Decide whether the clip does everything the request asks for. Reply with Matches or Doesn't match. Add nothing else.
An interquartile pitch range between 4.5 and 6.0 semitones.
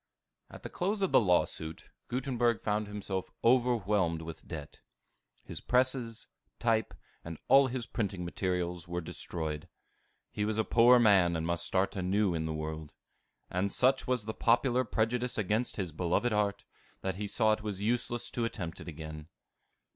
Matches